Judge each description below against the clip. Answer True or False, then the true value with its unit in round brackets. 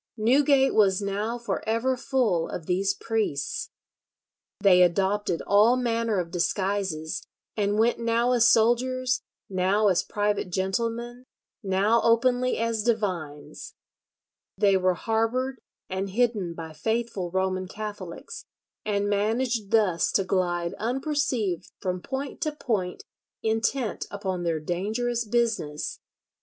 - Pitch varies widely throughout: False (4.0 semitones)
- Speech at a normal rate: False (120 wpm)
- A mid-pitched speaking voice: False (210 Hz)